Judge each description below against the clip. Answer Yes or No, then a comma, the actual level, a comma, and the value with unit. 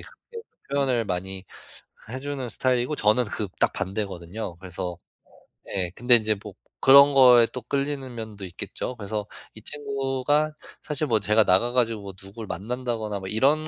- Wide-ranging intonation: No, average, 5.0 semitones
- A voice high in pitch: No, low, 115 Hz